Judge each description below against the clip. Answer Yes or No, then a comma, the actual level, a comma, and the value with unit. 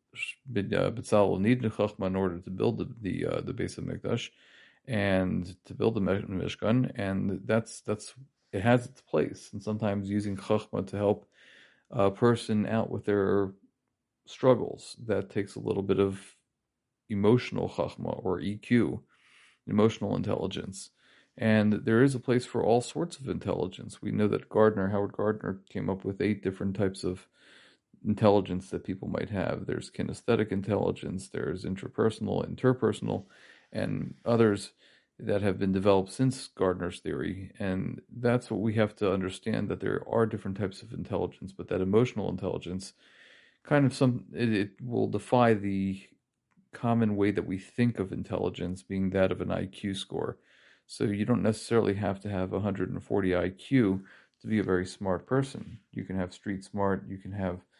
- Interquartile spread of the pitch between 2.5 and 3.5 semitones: Yes, average, 2.8 semitones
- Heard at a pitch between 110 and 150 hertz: No, low, 100 Hz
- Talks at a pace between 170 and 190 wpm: No, average, 160 wpm